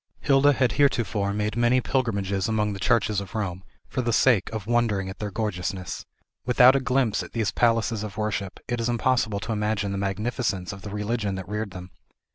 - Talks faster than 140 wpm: Yes, average, 195 wpm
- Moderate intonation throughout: Yes, average, 3.1 semitones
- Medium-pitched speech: No, low, 105 Hz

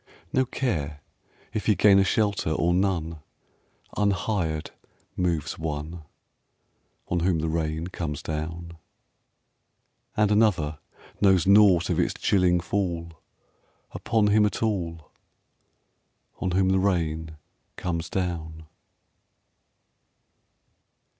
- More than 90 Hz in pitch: No, very low, 85 Hz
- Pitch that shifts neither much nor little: Yes, average, 3.7 semitones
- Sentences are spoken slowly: Yes, slow, 100 wpm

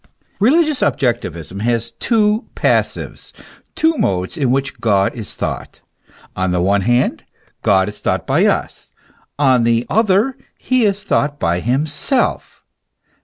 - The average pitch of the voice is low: Yes, low, 125 Hz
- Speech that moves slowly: Yes, slow, 130 wpm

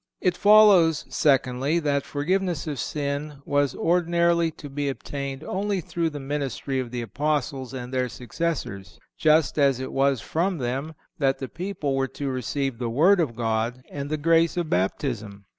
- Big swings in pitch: No, average, 4.0 semitones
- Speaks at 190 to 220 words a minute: No, average, 165 wpm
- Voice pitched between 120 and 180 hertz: Yes, medium, 140 Hz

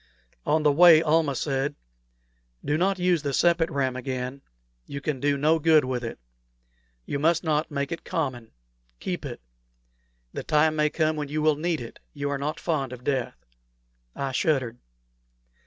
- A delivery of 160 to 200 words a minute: Yes, average, 170 wpm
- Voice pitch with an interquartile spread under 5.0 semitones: Yes, average, 2.7 semitones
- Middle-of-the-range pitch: Yes, medium, 150 Hz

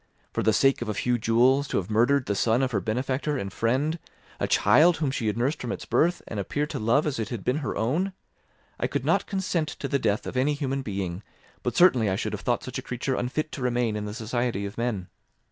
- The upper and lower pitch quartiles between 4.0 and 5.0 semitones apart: Yes, average, 4.4 semitones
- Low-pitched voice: Yes, low, 125 Hz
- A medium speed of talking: No, fast, 250 wpm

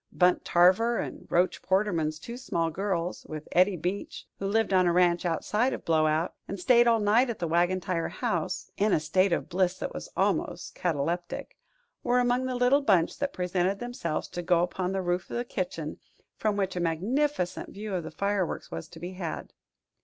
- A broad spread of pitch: No, average, 3.6 semitones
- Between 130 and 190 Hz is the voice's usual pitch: Yes, medium, 185 Hz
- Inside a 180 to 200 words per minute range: Yes, average, 195 wpm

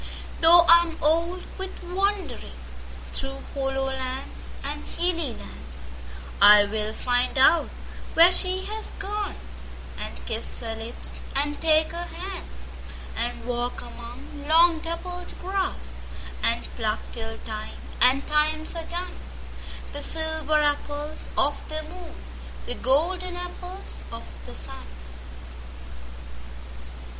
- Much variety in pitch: Yes, wide, 6.3 semitones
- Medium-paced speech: No, slow, 105 wpm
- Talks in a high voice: Yes, very high, 305 Hz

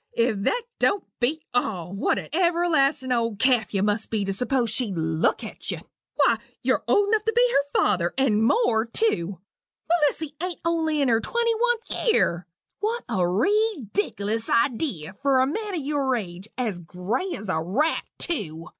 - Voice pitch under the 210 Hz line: No, very high, 255 Hz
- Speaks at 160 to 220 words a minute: Yes, average, 170 wpm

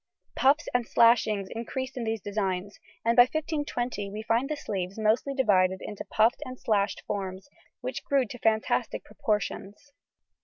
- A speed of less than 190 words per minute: Yes, average, 150 wpm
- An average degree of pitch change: Yes, average, 3.8 semitones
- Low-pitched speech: No, high, 220 Hz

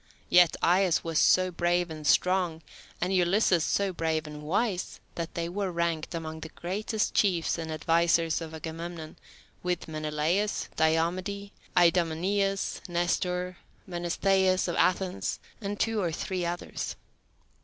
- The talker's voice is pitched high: No, medium, 175 Hz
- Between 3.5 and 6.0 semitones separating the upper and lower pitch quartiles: No, narrow, 2.4 semitones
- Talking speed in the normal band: No, slow, 130 wpm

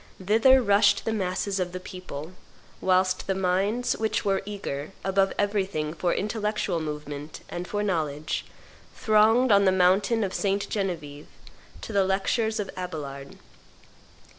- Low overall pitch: No, high, 190 Hz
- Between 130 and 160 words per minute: Yes, average, 140 wpm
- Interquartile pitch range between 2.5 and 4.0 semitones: Yes, average, 2.9 semitones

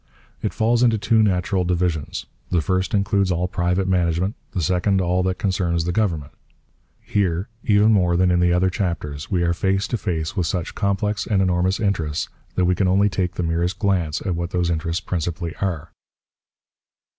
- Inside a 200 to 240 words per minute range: No, average, 180 wpm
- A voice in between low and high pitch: No, very low, 90 Hz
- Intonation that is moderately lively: No, narrow, 2.3 semitones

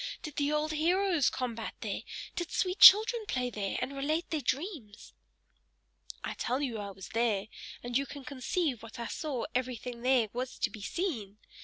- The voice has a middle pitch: No, very high, 260 Hz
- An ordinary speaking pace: Yes, average, 175 wpm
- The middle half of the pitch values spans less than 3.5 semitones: No, average, 5.1 semitones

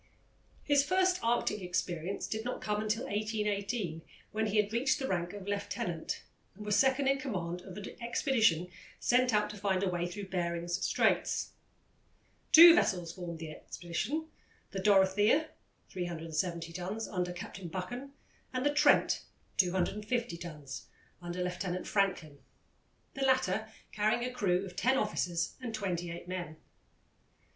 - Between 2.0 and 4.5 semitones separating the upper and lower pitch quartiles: No, average, 4.9 semitones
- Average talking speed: Yes, average, 145 wpm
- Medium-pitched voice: No, high, 200 Hz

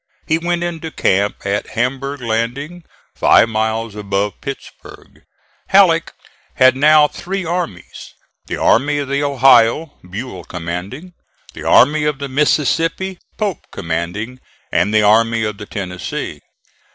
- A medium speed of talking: No, slow, 125 wpm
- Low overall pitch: Yes, low, 130 Hz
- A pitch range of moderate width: No, wide, 6.2 semitones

